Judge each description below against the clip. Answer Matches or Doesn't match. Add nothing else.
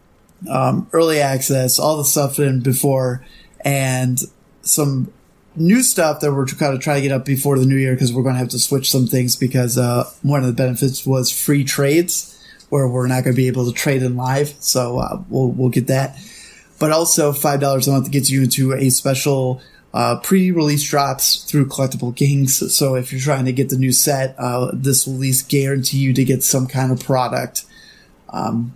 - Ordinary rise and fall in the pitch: Doesn't match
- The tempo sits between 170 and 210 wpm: Matches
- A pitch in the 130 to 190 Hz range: Matches